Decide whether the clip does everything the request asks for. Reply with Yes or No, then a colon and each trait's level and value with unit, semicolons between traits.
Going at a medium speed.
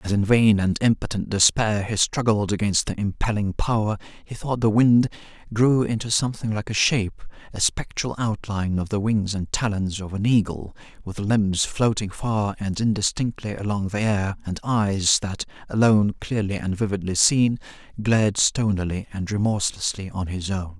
Yes: average, 160 wpm